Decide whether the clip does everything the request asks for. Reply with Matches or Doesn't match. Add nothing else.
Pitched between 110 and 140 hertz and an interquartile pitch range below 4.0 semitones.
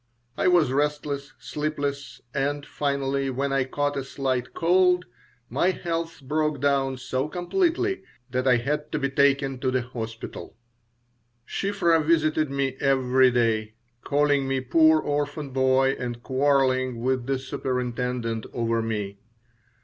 Matches